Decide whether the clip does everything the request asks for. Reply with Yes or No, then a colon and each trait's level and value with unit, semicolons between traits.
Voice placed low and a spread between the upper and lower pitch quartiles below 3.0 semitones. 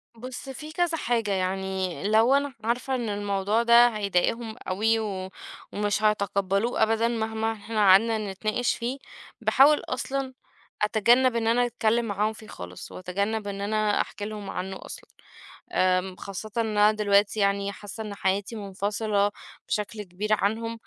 No: high, 215 Hz; narrow, 2.5 semitones